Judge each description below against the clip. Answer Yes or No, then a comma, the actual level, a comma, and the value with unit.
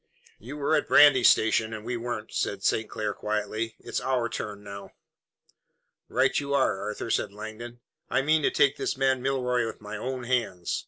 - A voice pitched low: Yes, low, 120 Hz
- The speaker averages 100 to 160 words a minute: No, average, 180 wpm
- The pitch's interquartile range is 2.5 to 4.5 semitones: Yes, average, 3.5 semitones